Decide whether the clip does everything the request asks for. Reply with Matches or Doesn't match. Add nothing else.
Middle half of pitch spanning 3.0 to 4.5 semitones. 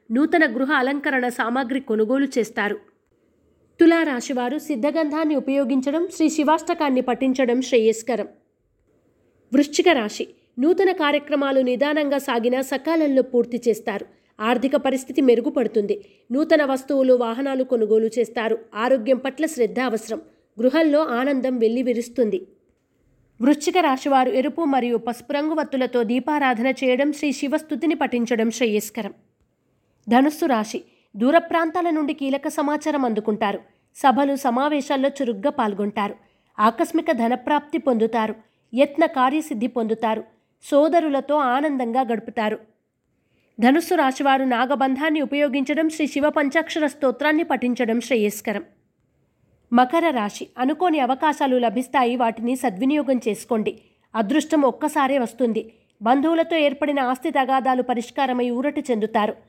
Matches